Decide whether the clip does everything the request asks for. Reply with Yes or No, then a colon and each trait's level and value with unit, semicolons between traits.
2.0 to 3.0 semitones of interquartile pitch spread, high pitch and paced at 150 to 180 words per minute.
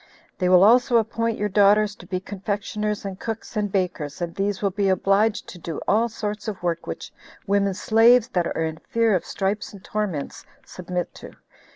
No: narrow, 2.6 semitones; high, 200 Hz; average, 190 wpm